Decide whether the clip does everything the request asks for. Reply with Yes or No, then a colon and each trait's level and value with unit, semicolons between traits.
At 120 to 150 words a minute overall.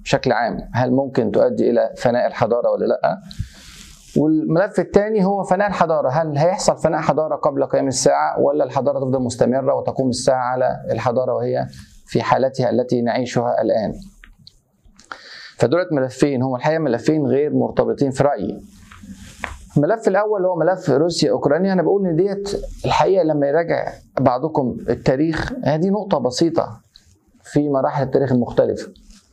Yes: fast, 135 wpm